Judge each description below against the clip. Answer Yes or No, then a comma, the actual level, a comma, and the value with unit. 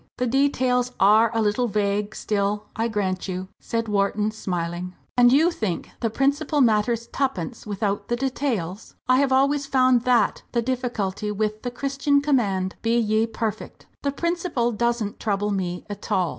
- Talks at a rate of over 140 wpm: Yes, average, 160 wpm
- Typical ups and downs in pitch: Yes, average, 4.0 semitones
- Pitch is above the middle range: Yes, high, 225 Hz